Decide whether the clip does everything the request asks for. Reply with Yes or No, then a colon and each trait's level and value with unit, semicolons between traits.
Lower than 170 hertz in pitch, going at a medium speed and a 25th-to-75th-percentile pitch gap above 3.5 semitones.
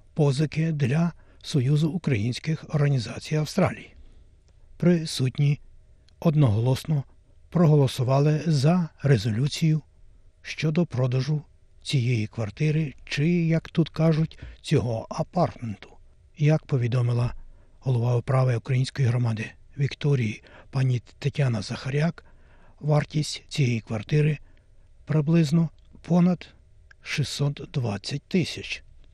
No: medium, 140 Hz; slow, 80 wpm; average, 5.0 semitones